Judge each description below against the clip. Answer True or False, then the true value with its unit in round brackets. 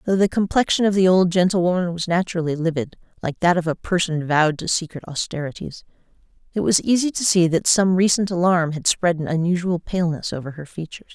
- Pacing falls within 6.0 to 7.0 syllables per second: True (6.1 syllables/s)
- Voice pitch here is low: False (175 Hz)